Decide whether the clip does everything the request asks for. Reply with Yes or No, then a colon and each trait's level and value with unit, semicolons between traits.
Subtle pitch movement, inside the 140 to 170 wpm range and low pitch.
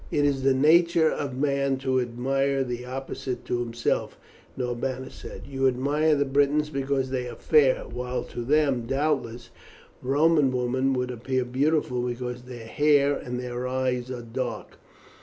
Yes: narrow, 2.2 semitones; average, 155 wpm; low, 130 Hz